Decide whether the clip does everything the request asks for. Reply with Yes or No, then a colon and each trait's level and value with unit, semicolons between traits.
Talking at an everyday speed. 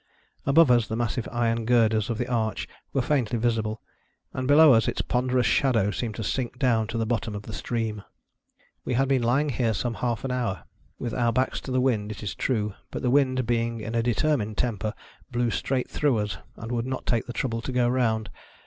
No: fast, 215 wpm